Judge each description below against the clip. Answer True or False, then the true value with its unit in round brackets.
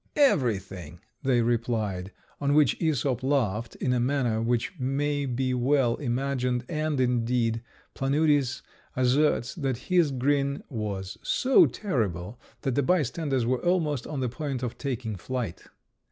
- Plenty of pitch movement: False (3.5 semitones)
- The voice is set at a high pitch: False (130 Hz)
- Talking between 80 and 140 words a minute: True (135 wpm)